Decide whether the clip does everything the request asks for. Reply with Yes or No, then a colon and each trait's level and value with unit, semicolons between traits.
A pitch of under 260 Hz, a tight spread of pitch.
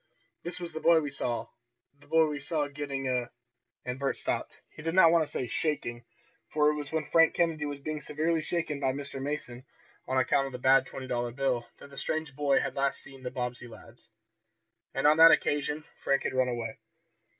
No: medium, 140 Hz; average, 3.0 semitones